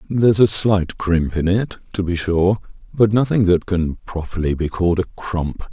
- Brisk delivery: No, average, 190 wpm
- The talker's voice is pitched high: No, very low, 95 Hz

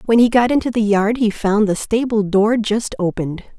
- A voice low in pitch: No, high, 215 Hz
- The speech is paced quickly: Yes, fast, 220 wpm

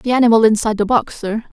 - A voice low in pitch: No, high, 225 Hz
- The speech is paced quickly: Yes, fast, 225 wpm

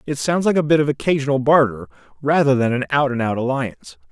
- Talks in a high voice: No, low, 135 Hz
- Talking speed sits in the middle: No, fast, 220 wpm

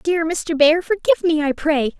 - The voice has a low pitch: No, very high, 310 Hz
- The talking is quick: Yes, fast, 210 wpm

